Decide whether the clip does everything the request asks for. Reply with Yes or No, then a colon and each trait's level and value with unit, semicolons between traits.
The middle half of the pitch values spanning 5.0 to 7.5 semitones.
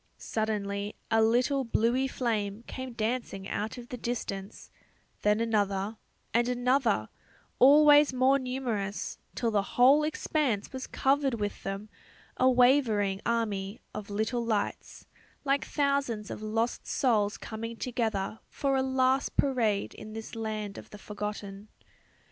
No: average, 3.8 semitones